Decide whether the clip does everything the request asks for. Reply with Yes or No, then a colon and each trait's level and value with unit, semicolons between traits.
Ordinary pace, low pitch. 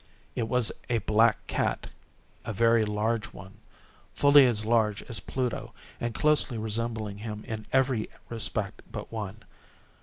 No: slow, 125 wpm; low, 110 Hz